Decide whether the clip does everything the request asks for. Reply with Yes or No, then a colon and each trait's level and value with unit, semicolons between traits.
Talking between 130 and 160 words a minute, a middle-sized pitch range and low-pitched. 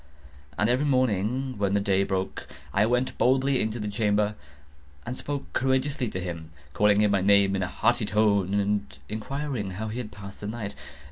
No: average, 185 wpm; average, 3.9 semitones; low, 105 Hz